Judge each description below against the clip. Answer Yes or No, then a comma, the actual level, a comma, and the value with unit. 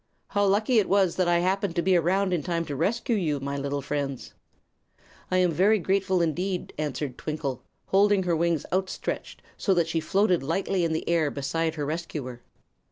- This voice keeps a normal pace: Yes, average, 185 wpm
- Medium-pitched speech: Yes, medium, 170 Hz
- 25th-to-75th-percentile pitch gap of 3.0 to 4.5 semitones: Yes, average, 4.1 semitones